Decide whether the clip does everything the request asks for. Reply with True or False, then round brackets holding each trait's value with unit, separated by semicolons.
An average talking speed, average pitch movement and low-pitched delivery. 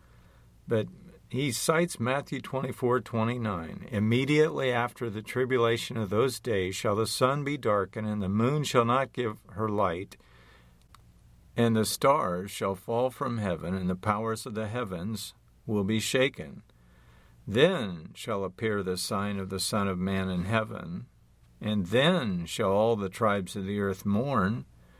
True (150 wpm; 4.3 semitones; 110 Hz)